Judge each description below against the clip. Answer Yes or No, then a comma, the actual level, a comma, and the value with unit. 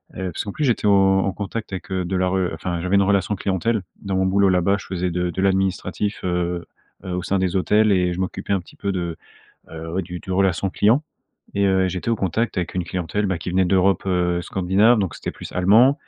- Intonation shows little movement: Yes, narrow, 1.8 semitones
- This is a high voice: No, very low, 95 Hz